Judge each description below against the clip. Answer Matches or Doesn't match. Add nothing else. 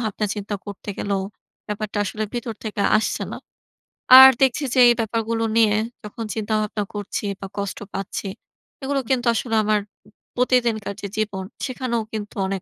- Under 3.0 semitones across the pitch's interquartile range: Matches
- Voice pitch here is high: Matches